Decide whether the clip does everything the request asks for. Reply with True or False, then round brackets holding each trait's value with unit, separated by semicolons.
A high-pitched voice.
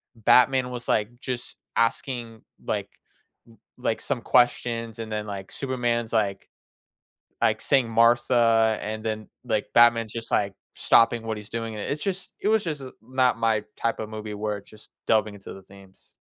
False (115 Hz)